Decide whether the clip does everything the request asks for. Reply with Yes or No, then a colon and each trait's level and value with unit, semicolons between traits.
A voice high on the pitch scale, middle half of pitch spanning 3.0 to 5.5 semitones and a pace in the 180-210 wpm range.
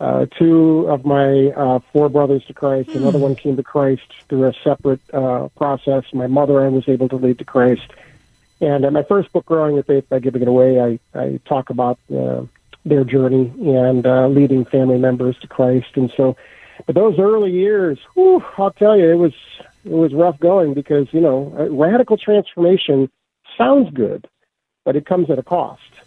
No: medium, 140 Hz; average, 3.9 semitones; average, 195 wpm